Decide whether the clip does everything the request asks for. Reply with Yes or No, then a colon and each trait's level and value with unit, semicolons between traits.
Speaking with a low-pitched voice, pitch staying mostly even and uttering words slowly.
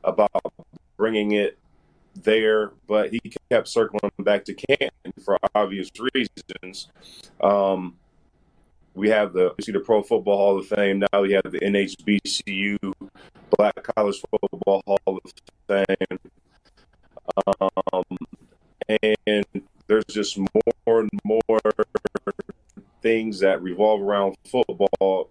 Yes: low, 100 Hz; narrow, 1.9 semitones; slow, 115 wpm